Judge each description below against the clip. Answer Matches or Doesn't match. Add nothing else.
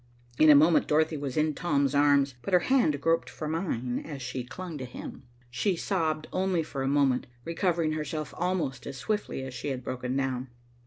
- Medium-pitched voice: Matches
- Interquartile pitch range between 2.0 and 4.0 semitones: Matches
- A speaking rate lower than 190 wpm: Doesn't match